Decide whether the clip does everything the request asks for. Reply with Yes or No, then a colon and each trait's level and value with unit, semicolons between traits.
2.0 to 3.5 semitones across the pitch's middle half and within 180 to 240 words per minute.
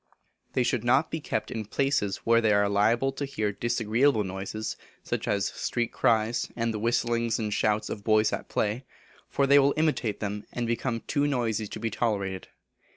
Yes: average, 2.7 semitones; average, 185 wpm